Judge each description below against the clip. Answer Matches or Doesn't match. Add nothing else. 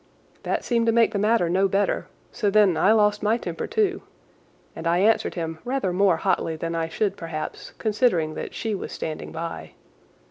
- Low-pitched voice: Doesn't match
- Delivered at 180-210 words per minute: Matches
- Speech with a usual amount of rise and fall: Matches